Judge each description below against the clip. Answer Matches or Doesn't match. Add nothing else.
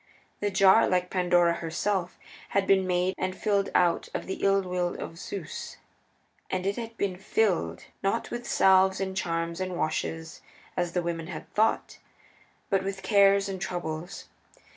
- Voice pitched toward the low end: Doesn't match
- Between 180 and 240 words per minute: Doesn't match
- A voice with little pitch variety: Matches